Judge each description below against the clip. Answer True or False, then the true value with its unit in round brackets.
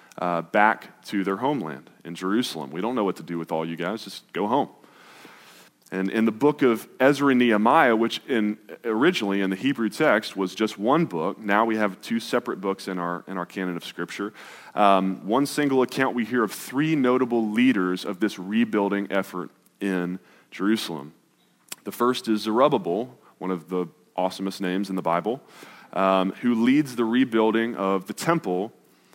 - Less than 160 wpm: False (180 wpm)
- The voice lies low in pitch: True (100 Hz)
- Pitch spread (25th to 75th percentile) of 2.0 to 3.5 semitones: False (3.9 semitones)